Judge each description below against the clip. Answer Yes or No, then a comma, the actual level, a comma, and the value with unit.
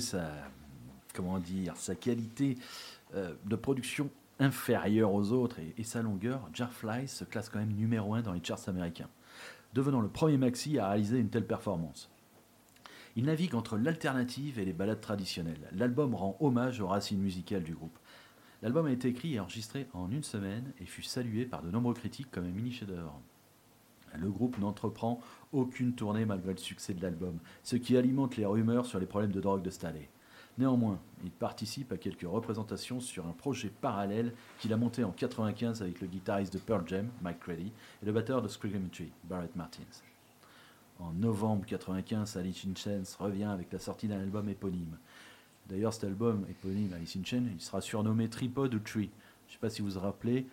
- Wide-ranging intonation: No, average, 4.2 semitones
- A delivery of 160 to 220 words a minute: Yes, average, 190 wpm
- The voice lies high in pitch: No, low, 105 Hz